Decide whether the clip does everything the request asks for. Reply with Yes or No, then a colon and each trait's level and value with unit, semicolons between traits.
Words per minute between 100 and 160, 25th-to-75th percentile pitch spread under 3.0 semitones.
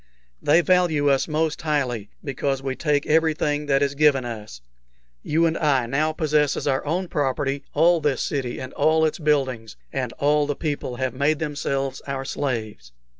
No: average, 175 wpm; narrow, 2.4 semitones